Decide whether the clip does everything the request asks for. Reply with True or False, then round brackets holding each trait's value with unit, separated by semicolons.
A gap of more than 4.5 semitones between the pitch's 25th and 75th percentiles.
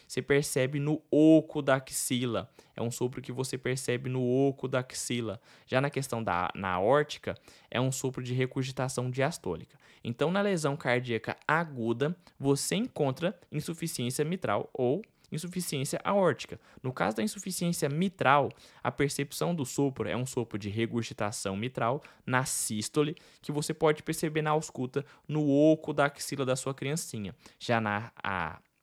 False (3.7 semitones)